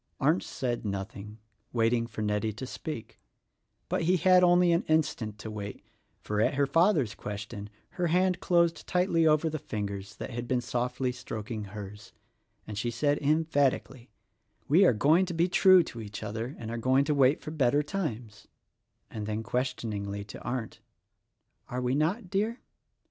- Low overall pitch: Yes, low, 125 Hz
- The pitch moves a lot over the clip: Yes, wide, 6.8 semitones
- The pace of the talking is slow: No, average, 165 wpm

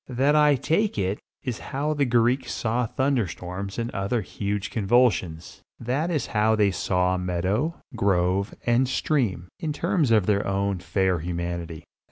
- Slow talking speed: No, average, 155 wpm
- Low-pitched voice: Yes, low, 105 Hz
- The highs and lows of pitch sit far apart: Yes, wide, 5.8 semitones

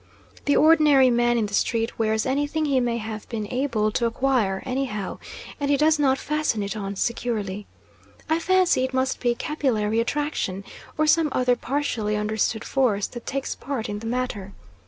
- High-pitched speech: Yes, high, 245 Hz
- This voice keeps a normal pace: Yes, average, 175 wpm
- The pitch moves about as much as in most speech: Yes, average, 4.6 semitones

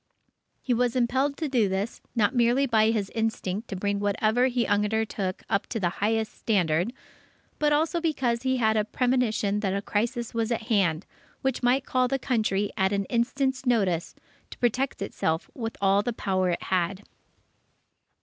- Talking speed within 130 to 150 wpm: No, average, 170 wpm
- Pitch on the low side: No, high, 225 Hz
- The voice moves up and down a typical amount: Yes, average, 3.8 semitones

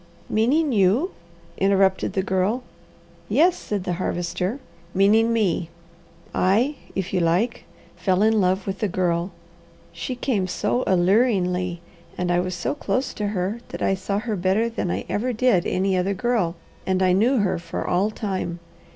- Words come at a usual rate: Yes, average, 160 wpm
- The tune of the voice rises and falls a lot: No, average, 3.7 semitones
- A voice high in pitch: Yes, high, 195 Hz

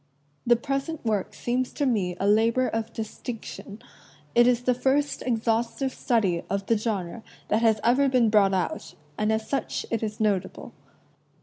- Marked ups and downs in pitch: No, average, 3.0 semitones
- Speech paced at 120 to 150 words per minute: No, average, 165 wpm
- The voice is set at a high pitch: Yes, high, 225 Hz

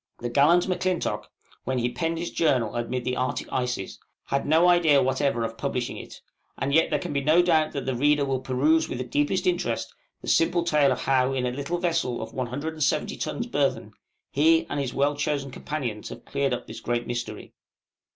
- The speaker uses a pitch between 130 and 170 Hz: Yes, medium, 140 Hz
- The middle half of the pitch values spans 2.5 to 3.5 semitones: No, average, 4.1 semitones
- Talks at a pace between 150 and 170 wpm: No, average, 200 wpm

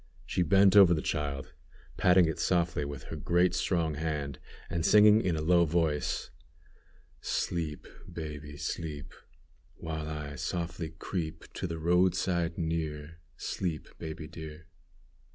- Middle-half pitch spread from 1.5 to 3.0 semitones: Yes, narrow, 2.4 semitones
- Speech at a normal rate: No, slow, 130 wpm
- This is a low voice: Yes, very low, 80 Hz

